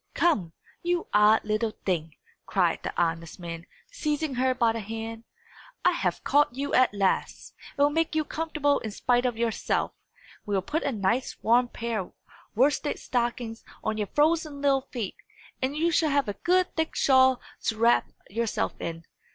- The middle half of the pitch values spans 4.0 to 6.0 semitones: Yes, average, 5.2 semitones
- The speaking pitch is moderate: No, high, 240 Hz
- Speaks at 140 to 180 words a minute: Yes, average, 175 wpm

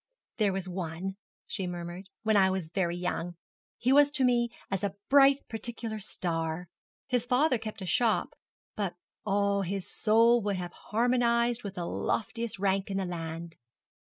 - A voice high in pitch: Yes, high, 200 Hz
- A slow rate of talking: No, average, 160 wpm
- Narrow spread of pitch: No, average, 4.7 semitones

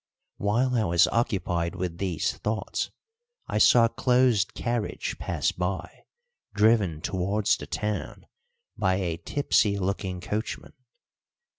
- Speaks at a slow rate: Yes, slow, 120 wpm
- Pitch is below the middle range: Yes, low, 100 Hz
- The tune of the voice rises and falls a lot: No, average, 3.8 semitones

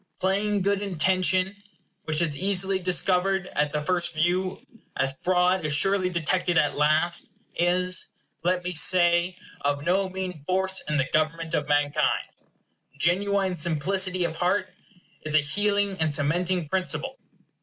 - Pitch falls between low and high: Yes, medium, 180 Hz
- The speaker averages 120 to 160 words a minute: Yes, average, 145 wpm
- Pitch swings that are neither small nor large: Yes, average, 3.3 semitones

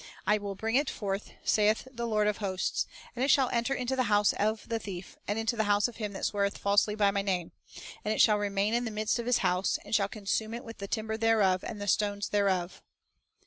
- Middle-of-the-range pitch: No, high, 210 Hz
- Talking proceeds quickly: Yes, fast, 240 wpm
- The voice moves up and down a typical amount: No, narrow, 2.0 semitones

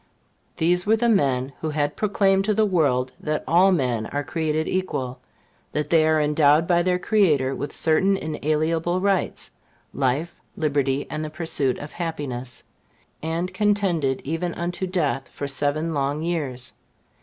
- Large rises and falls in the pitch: No, average, 3.9 semitones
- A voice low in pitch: No, medium, 155 Hz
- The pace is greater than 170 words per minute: No, average, 150 wpm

